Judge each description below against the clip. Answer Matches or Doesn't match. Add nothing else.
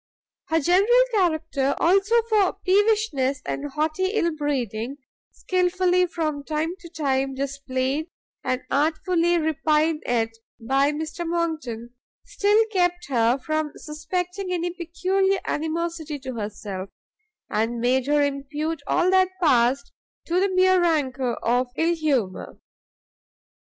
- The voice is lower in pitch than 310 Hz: Doesn't match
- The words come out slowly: Matches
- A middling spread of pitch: Matches